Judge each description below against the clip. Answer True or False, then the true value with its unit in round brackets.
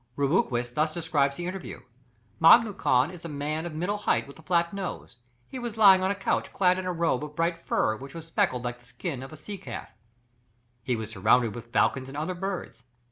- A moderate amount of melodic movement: False (5.7 semitones)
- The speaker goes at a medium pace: False (220 wpm)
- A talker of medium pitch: True (160 Hz)